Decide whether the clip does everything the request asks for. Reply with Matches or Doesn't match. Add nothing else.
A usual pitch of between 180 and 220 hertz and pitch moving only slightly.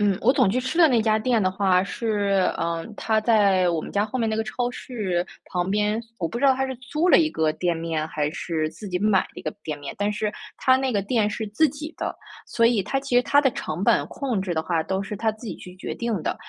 Doesn't match